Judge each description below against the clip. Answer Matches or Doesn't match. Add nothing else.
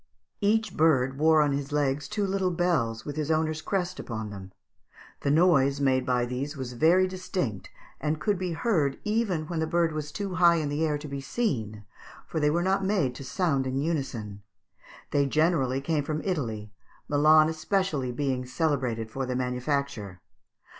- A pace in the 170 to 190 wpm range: Matches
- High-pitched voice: Doesn't match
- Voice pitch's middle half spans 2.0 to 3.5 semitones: Doesn't match